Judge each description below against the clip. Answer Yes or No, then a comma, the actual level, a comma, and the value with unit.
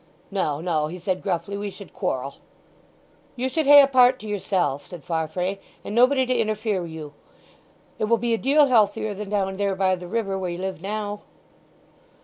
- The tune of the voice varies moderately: Yes, average, 4.2 semitones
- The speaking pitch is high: Yes, high, 200 Hz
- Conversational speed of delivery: Yes, average, 190 wpm